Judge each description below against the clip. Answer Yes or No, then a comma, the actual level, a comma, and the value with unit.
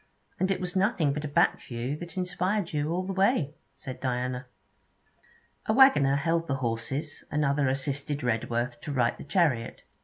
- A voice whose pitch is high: No, medium, 145 Hz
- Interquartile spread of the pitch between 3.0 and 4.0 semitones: No, wide, 5.6 semitones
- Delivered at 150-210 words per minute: Yes, average, 165 wpm